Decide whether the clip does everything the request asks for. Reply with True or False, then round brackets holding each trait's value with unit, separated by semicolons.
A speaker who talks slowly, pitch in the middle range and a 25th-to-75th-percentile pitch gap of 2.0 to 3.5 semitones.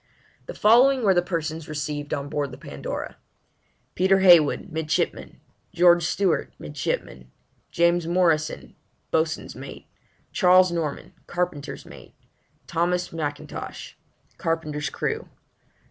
True (105 wpm; 165 Hz; 2.9 semitones)